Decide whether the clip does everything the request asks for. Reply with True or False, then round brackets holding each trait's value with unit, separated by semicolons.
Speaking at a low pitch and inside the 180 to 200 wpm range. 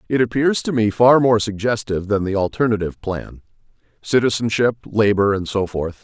False (110 Hz; 150 wpm)